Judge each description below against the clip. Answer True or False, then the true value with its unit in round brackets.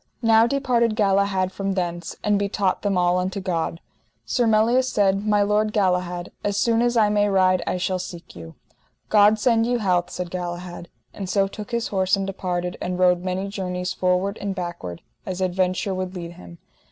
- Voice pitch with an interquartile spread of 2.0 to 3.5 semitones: True (2.4 semitones)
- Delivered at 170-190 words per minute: True (185 wpm)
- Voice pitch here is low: False (190 Hz)